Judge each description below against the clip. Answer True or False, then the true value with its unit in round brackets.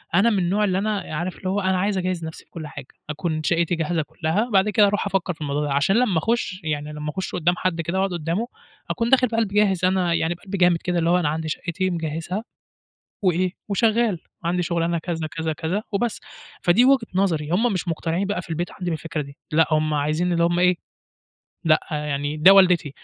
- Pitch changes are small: False (3.3 semitones)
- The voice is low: False (175 Hz)